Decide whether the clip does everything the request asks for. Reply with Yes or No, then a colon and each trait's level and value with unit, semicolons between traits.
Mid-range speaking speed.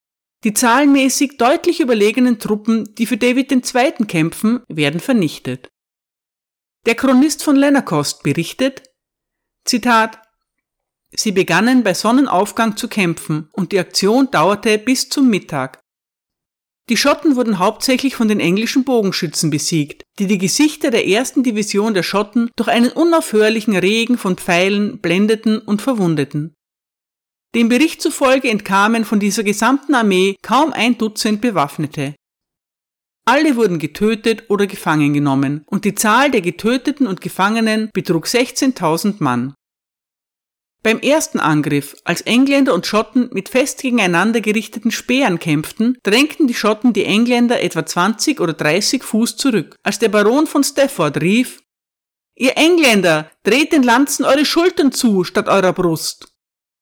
Yes: average, 135 wpm